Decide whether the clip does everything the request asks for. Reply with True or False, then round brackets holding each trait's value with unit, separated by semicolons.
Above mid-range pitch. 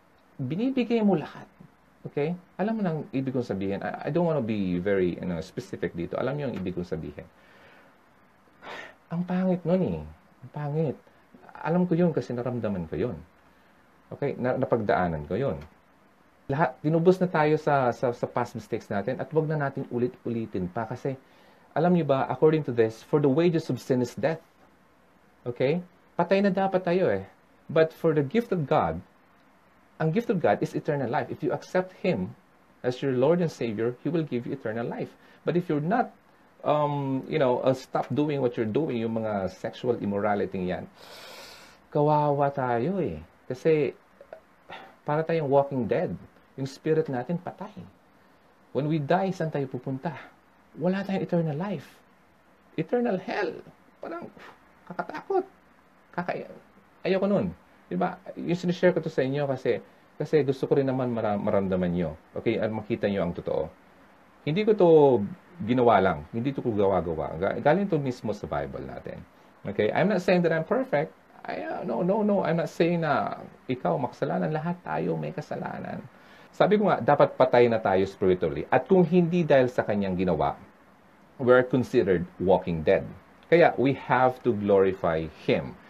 False (140 Hz)